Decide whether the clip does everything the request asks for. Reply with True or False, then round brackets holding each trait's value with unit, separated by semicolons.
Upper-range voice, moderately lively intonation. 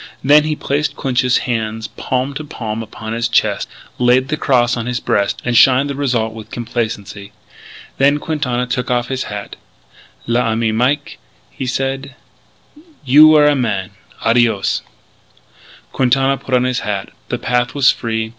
False (125 Hz; 3.2 semitones)